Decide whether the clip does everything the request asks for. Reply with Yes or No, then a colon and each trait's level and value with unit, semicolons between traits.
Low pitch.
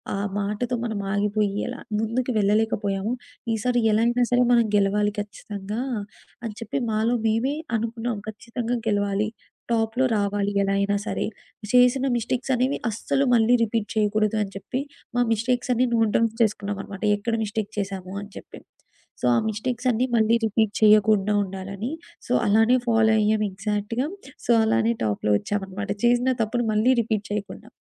No: high, 220 Hz